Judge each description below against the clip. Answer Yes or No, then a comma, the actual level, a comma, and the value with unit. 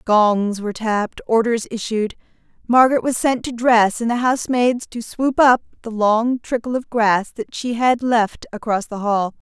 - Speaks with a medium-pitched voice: No, high, 230 Hz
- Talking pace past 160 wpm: Yes, average, 175 wpm